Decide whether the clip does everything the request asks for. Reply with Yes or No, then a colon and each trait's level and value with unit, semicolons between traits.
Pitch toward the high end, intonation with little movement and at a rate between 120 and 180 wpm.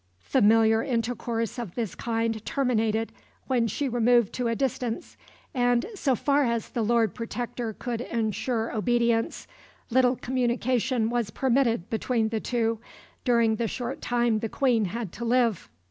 Yes: high, 235 Hz; narrow, 1.6 semitones; average, 145 wpm